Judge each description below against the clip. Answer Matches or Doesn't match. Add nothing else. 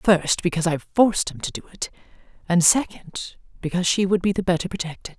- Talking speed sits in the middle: Matches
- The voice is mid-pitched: Matches